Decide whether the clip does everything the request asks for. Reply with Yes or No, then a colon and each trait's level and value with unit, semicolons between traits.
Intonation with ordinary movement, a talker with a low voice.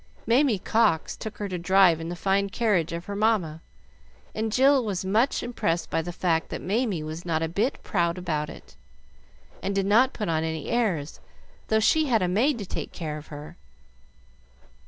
No: average, 5.0 semitones; high, 190 Hz